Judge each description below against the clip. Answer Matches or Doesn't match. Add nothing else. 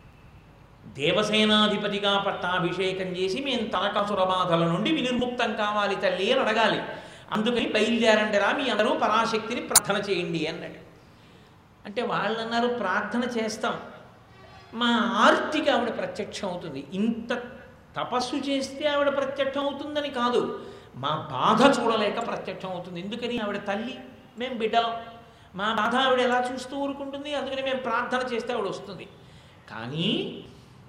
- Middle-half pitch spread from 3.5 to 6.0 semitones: Matches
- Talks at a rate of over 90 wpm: Matches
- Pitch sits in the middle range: Doesn't match